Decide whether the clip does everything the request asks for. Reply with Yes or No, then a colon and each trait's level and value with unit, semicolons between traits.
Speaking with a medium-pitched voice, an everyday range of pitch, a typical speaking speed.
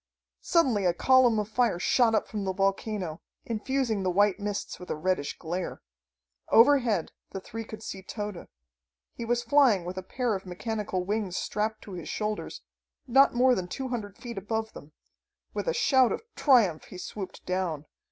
No: high, 210 Hz; average, 4.3 semitones; average, 175 wpm